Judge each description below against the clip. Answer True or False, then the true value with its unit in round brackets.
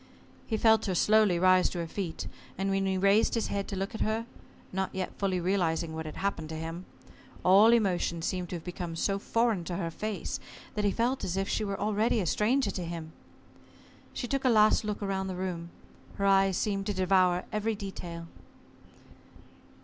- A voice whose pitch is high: True (195 Hz)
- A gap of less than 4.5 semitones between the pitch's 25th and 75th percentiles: True (3.1 semitones)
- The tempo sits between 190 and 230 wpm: True (195 wpm)